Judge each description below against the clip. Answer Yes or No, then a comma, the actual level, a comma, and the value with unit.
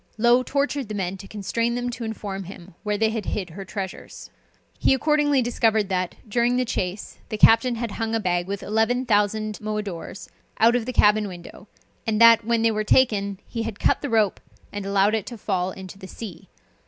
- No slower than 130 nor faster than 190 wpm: No, fast, 205 wpm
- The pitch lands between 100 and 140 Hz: No, high, 215 Hz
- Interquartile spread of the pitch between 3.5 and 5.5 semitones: No, average, 2.9 semitones